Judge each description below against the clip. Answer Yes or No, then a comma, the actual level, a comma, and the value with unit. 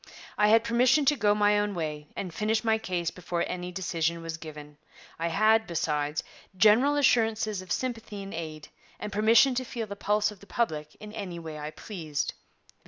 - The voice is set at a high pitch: Yes, high, 200 Hz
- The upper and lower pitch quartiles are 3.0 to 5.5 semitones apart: Yes, average, 5.1 semitones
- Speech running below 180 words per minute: No, average, 185 wpm